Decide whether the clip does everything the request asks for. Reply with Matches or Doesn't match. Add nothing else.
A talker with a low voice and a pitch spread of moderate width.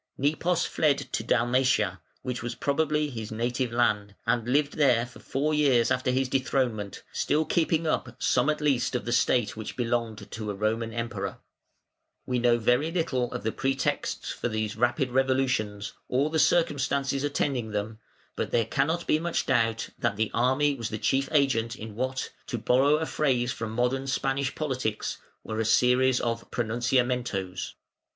Matches